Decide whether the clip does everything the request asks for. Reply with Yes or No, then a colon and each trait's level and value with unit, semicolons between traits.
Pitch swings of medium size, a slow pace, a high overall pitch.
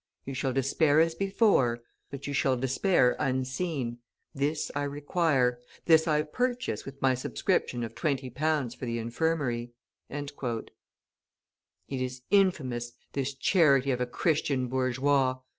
No: average, 3.5 semitones; slow, 130 wpm; low, 135 Hz